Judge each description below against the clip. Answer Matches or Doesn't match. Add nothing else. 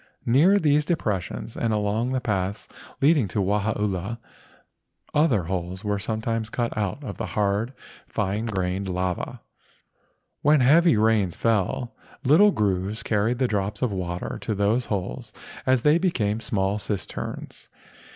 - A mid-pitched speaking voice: Doesn't match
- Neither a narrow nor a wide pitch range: Matches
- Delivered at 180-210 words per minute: Doesn't match